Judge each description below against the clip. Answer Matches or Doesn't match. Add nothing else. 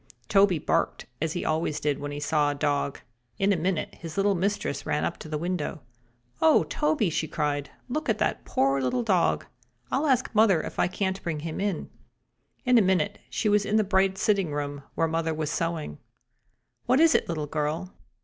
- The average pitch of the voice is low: Doesn't match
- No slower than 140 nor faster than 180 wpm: Doesn't match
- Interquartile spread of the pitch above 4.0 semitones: Matches